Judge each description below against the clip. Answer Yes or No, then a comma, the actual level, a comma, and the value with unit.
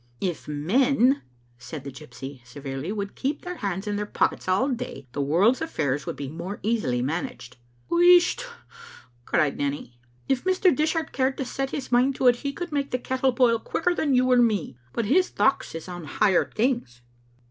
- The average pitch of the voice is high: Yes, high, 230 Hz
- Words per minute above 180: Yes, average, 190 wpm